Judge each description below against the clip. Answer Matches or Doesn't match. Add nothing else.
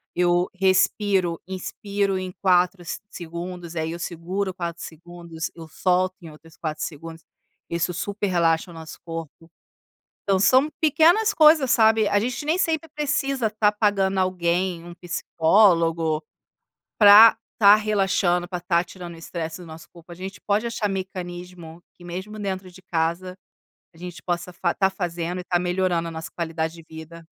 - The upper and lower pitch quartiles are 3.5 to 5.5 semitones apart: Doesn't match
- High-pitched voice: Doesn't match